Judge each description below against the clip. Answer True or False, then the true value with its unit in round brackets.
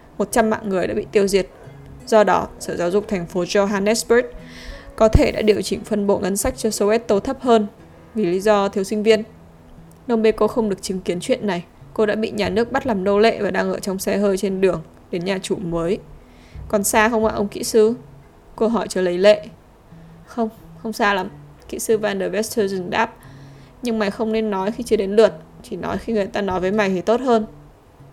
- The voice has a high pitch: True (205 Hz)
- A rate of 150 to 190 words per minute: False (225 wpm)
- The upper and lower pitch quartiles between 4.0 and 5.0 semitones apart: False (2.9 semitones)